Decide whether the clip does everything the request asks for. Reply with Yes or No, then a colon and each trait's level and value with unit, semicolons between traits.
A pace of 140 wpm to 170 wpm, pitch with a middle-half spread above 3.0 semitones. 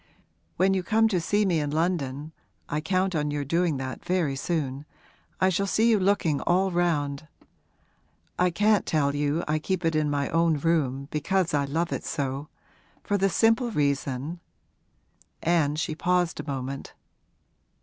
Yes: average, 165 wpm; average, 4.2 semitones